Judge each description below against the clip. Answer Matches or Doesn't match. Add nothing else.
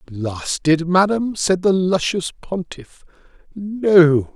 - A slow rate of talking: Matches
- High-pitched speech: Doesn't match